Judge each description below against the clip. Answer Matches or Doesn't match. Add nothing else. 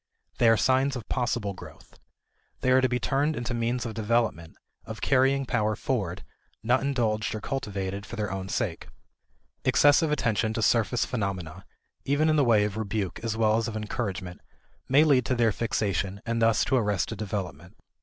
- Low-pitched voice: Matches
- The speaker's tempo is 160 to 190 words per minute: Matches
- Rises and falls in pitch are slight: Doesn't match